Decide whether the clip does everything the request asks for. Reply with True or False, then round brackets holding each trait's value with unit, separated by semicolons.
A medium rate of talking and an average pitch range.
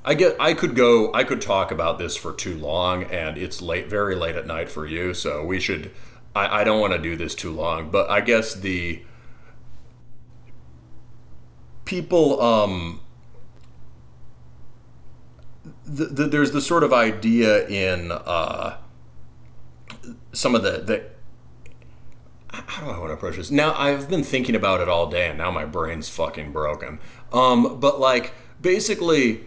False (155 wpm; 8.6 semitones)